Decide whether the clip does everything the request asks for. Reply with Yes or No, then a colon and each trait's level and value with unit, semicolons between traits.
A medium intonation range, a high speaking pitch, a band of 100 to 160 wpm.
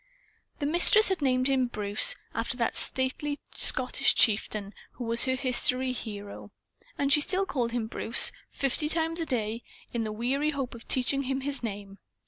No: average, 3.7 semitones; very high, 255 Hz; average, 170 wpm